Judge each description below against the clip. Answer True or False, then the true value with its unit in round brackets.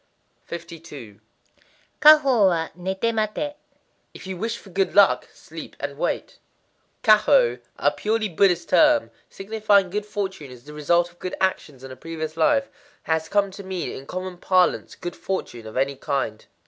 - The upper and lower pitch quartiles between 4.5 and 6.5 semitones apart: True (4.9 semitones)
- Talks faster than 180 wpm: False (155 wpm)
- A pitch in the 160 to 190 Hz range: True (185 Hz)